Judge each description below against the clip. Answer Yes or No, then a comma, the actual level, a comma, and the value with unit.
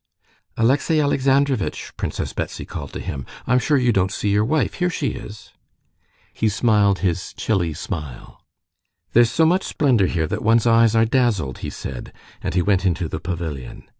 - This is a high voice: No, low, 110 Hz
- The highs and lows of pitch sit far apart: Yes, wide, 5.9 semitones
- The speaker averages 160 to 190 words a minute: Yes, average, 170 wpm